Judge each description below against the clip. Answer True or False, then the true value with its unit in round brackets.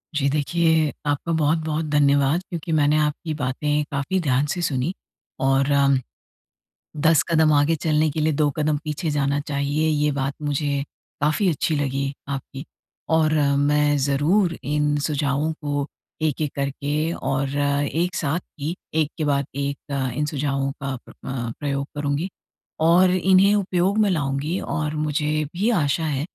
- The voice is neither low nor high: True (150 Hz)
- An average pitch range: False (2.1 semitones)